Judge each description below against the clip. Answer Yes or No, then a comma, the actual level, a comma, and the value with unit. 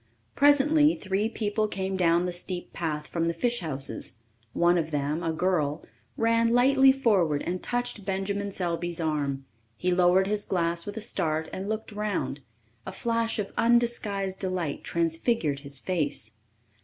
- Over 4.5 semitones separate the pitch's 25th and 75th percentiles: Yes, average, 4.9 semitones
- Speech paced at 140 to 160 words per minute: Yes, average, 155 wpm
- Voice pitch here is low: No, medium, 185 Hz